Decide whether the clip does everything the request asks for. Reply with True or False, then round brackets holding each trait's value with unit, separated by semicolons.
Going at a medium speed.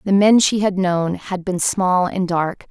False (220 wpm)